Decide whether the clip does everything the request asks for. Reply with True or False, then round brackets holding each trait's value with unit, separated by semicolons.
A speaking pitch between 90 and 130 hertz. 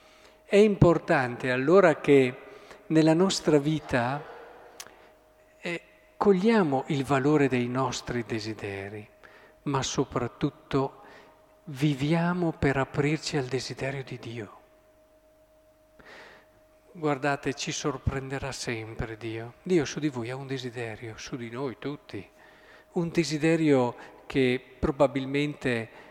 False (140 Hz)